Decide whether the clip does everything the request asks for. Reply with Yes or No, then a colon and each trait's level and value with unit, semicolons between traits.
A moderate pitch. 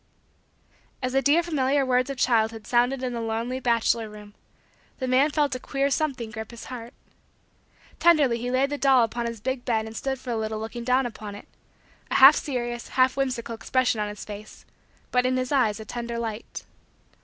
No: high, 245 Hz